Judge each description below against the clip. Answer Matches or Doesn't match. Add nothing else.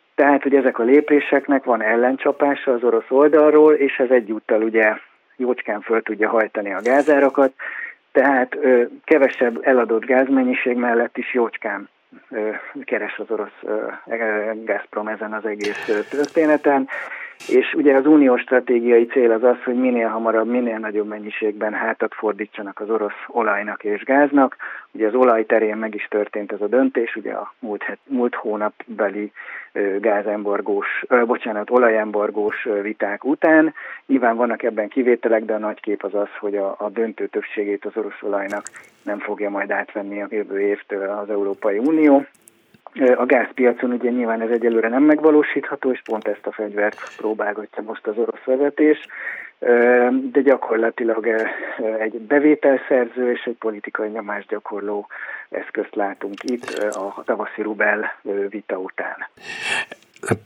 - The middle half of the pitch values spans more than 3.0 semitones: Matches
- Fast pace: Doesn't match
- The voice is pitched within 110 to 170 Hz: Matches